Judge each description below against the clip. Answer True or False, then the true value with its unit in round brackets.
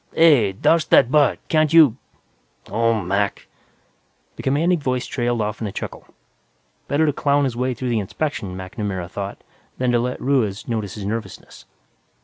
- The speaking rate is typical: True (160 wpm)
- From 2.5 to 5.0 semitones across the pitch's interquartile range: False (5.5 semitones)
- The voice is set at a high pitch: False (120 Hz)